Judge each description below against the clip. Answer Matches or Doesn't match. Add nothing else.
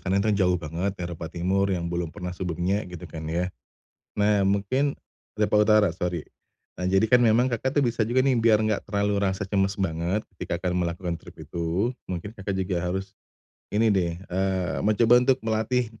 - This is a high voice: Doesn't match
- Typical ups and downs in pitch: Matches